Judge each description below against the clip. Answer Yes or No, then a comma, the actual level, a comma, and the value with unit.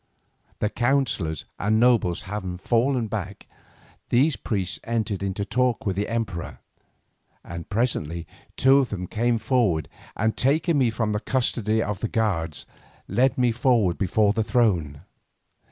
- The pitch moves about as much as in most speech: Yes, average, 4.2 semitones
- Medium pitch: No, low, 110 Hz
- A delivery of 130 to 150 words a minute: Yes, average, 140 wpm